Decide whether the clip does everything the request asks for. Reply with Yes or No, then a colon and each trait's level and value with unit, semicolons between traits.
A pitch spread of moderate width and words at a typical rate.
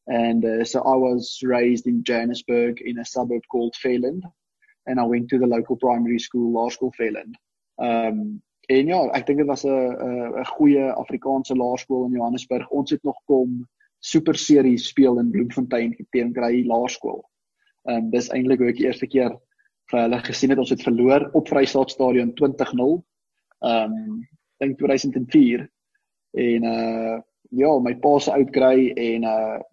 No: narrow, 2.3 semitones; average, 170 wpm